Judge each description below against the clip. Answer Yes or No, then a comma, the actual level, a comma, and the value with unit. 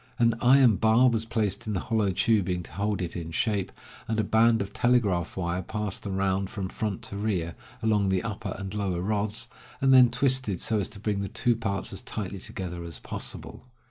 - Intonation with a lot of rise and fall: No, average, 2.8 semitones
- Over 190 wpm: Yes, fast, 205 wpm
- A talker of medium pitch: No, low, 105 Hz